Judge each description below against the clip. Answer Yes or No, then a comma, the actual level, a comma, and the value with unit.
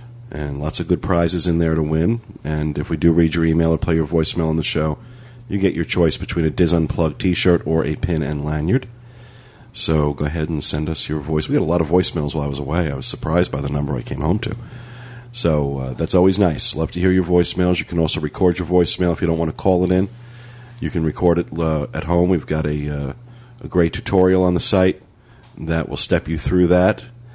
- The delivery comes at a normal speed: No, fast, 245 wpm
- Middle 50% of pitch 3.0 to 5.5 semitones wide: Yes, average, 3.4 semitones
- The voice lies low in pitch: Yes, very low, 85 Hz